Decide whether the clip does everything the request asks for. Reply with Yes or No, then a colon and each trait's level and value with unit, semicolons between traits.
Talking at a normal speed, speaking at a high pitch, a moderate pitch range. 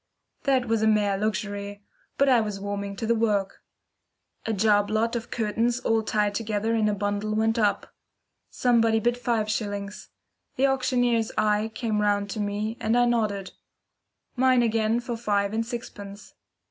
No: average, 160 wpm; high, 220 Hz; narrow, 2.3 semitones